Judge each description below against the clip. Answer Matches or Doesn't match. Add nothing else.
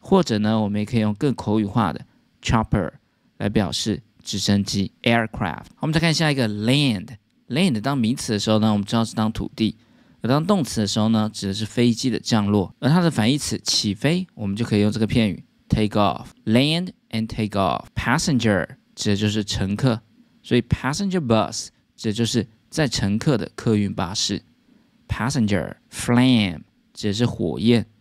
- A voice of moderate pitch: Doesn't match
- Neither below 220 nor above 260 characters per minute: Doesn't match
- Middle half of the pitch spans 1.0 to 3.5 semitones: Matches